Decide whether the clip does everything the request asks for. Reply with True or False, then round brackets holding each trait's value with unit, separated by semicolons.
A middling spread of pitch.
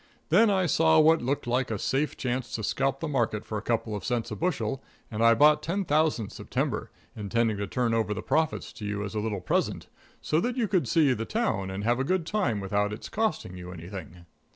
False (7.0 semitones)